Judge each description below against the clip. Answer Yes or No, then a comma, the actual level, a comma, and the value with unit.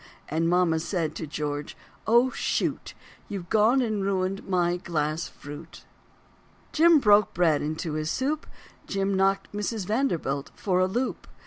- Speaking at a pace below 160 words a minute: Yes, average, 140 wpm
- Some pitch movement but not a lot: Yes, average, 4.7 semitones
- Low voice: No, medium, 185 Hz